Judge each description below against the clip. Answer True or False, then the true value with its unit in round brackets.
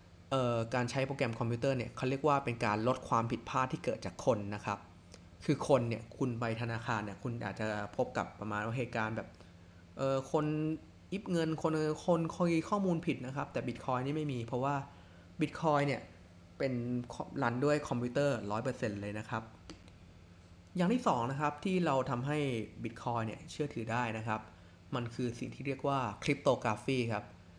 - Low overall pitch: True (120 Hz)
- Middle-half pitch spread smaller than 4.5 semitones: False (4.9 semitones)